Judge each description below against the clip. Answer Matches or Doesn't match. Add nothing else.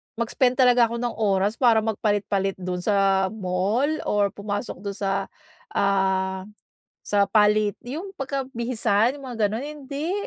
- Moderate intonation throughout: Matches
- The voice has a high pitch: Matches